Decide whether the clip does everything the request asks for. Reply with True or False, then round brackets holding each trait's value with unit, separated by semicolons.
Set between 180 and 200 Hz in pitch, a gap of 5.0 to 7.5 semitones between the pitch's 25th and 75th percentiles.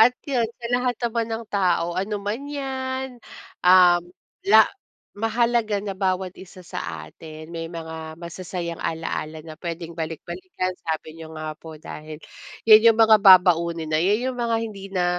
True (185 Hz; 5.4 semitones)